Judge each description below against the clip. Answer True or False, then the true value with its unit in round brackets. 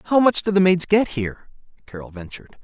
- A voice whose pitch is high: False (165 Hz)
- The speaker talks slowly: False (205 wpm)